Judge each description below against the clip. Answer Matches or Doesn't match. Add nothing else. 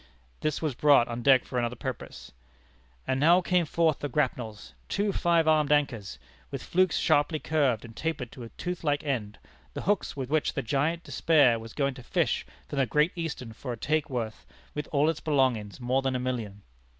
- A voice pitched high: Doesn't match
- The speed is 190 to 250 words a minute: Matches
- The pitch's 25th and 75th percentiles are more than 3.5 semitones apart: Matches